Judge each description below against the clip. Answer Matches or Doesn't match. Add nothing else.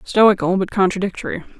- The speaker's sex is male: Doesn't match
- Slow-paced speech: Matches